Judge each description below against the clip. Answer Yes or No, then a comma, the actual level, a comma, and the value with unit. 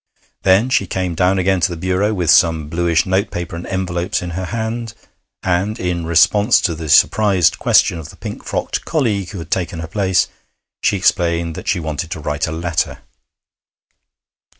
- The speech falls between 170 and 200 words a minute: Yes, average, 180 wpm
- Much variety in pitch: No, average, 2.7 semitones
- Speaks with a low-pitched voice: Yes, very low, 90 Hz